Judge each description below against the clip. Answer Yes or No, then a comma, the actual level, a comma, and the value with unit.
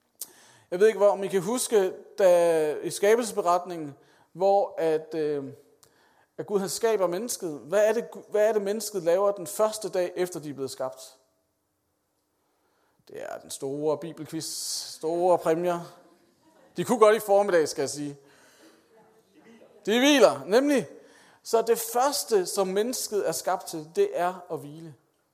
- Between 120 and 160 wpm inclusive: Yes, average, 150 wpm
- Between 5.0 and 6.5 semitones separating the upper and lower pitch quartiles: Yes, average, 5.3 semitones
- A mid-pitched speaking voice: Yes, medium, 180 Hz